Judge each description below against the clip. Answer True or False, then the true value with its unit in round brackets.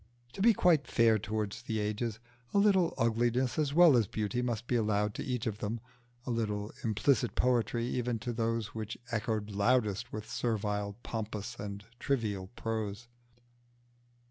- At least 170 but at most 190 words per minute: False (155 wpm)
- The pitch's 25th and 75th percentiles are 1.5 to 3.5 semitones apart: True (2.7 semitones)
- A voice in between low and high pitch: False (115 Hz)